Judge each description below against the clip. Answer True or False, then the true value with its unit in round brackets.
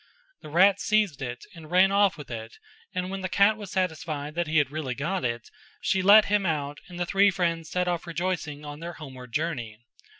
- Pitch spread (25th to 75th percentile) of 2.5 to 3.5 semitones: False (4.3 semitones)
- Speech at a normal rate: False (210 wpm)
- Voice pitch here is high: False (170 Hz)